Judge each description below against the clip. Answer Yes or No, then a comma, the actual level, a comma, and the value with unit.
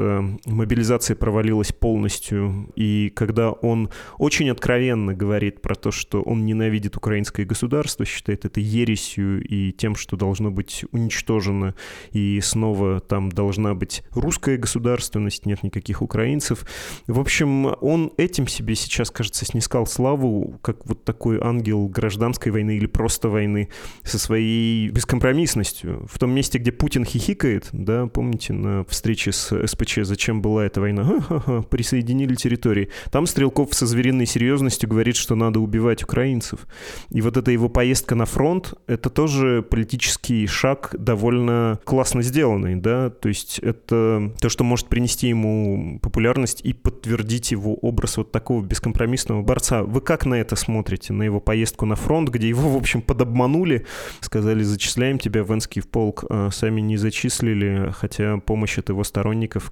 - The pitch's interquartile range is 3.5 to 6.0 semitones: No, average, 2.9 semitones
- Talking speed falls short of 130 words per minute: No, average, 150 wpm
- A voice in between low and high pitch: No, low, 115 Hz